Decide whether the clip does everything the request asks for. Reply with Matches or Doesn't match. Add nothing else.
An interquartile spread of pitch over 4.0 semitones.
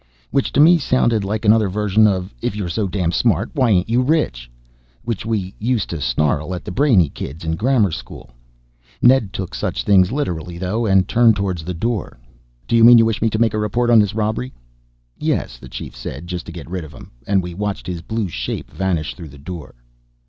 Matches